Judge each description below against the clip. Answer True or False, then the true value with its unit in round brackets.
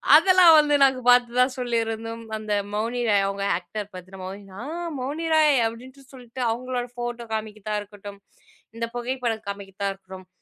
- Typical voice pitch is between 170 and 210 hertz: False (230 Hz)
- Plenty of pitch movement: False (3.7 semitones)